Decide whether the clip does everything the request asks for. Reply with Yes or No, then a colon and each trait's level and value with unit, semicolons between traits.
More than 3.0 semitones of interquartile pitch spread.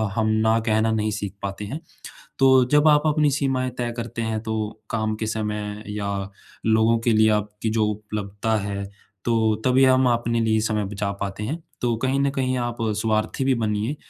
No: narrow, 2.5 semitones